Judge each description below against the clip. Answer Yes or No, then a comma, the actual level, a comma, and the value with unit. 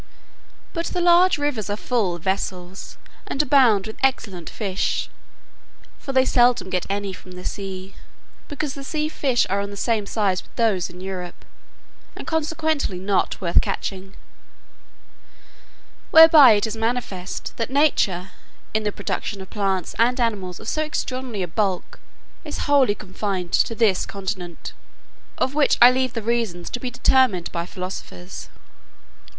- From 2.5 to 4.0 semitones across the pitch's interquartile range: No, wide, 5.6 semitones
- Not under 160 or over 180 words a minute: No, average, 150 wpm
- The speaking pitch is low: No, high, 210 Hz